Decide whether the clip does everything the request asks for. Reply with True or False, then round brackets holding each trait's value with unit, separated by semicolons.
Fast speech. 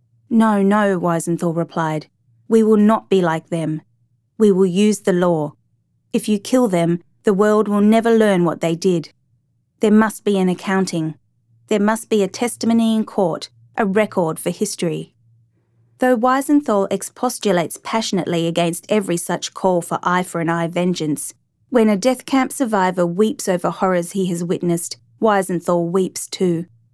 False (160 wpm)